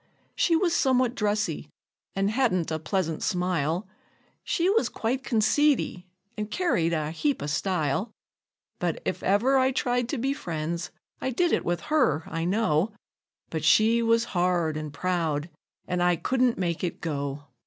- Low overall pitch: No, high, 190 Hz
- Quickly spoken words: No, average, 155 wpm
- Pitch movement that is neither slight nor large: No, wide, 7.1 semitones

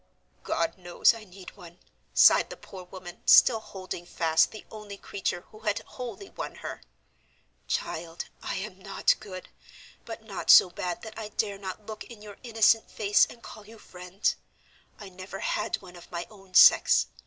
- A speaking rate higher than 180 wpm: No, average, 175 wpm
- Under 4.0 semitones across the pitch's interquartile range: Yes, average, 3.0 semitones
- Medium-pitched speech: No, high, 195 Hz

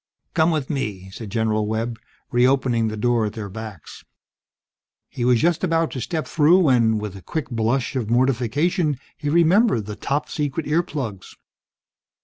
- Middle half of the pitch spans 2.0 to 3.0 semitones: No, wide, 5.6 semitones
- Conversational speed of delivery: Yes, average, 160 wpm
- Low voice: Yes, low, 125 Hz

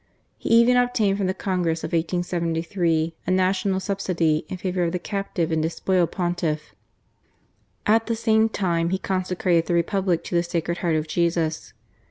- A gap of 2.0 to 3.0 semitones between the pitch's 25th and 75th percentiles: Yes, narrow, 2.5 semitones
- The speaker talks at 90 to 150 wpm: No, average, 165 wpm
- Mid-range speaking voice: Yes, medium, 175 Hz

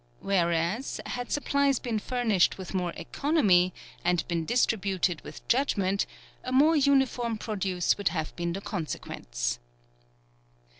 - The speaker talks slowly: Yes, slow, 120 wpm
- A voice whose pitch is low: No, high, 195 Hz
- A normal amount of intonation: No, wide, 6.0 semitones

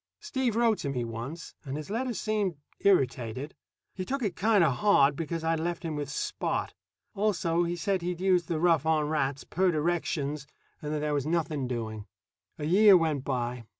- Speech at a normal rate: Yes, average, 185 wpm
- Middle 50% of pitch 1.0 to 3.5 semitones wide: No, average, 4.7 semitones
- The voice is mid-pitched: Yes, medium, 160 Hz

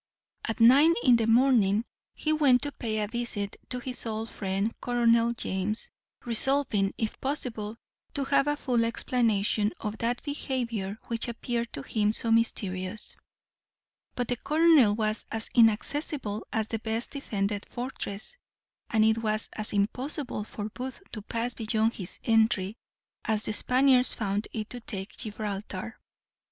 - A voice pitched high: Yes, high, 225 Hz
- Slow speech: No, average, 145 wpm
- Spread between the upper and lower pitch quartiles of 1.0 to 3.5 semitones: Yes, average, 2.8 semitones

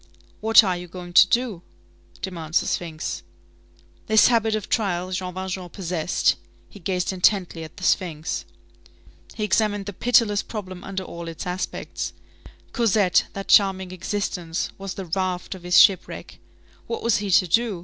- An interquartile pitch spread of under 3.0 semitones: Yes, narrow, 2.5 semitones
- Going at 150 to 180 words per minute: Yes, average, 155 wpm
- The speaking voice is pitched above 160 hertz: Yes, high, 190 Hz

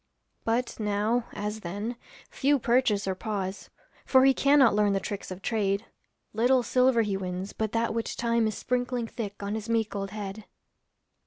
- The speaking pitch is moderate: No, high, 220 Hz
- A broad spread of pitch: No, average, 3.0 semitones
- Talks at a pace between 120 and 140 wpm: No, average, 170 wpm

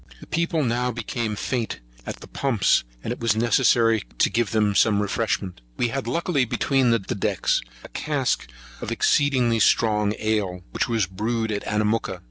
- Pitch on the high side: No, low, 115 Hz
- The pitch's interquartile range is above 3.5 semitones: No, average, 2.7 semitones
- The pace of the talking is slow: No, average, 160 wpm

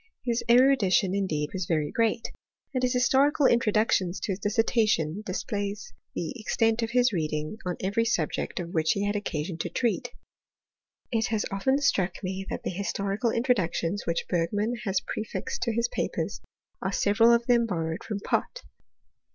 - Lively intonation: No, average, 4.3 semitones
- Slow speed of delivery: No, average, 165 wpm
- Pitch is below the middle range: No, high, 205 Hz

